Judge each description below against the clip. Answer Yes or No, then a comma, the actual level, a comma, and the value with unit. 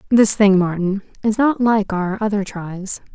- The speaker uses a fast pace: No, average, 170 wpm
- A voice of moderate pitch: No, high, 205 Hz